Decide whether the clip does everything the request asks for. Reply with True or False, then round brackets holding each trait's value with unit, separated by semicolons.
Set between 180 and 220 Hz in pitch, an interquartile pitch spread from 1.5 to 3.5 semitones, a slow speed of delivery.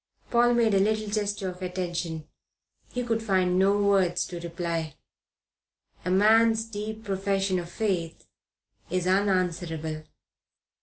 True (190 Hz; 3.2 semitones; 120 wpm)